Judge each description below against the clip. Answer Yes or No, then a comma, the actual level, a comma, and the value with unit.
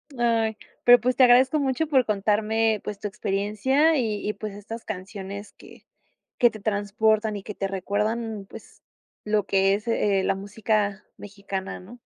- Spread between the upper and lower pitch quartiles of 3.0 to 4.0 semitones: No, narrow, 2.4 semitones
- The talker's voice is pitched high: Yes, high, 210 Hz